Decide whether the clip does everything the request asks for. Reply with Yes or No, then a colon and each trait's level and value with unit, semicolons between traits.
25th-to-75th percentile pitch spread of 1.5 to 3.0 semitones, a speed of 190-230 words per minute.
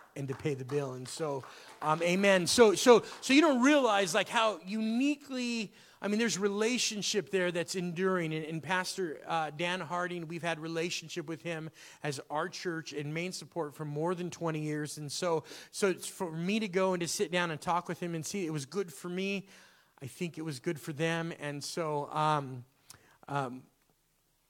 No: average, 3.9 semitones; average, 200 wpm